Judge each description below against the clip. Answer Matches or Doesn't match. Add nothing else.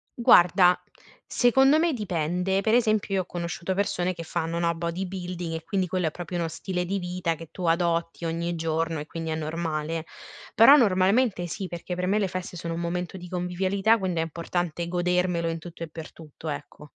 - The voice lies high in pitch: Doesn't match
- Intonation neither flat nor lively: Doesn't match